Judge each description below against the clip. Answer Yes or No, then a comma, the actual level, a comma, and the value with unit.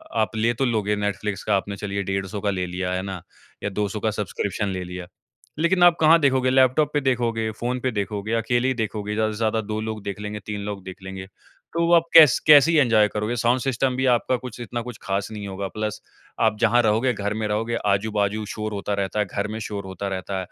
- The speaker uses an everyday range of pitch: Yes, average, 3.1 semitones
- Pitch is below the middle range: Yes, low, 105 Hz